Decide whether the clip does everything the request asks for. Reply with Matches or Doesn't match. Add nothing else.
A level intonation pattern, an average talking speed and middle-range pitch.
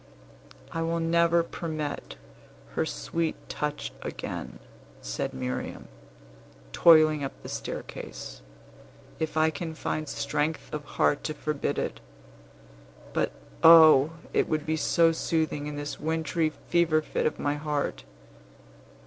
Doesn't match